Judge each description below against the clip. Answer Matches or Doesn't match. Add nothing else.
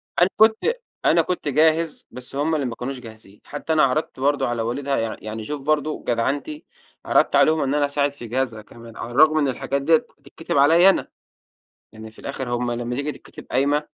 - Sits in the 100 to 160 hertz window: Matches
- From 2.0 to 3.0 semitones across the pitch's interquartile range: Doesn't match